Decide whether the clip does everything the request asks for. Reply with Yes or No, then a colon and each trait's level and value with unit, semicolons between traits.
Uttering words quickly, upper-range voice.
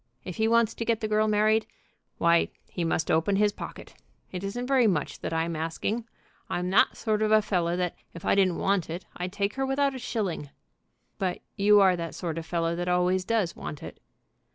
Yes: fast, 210 wpm; high, 195 Hz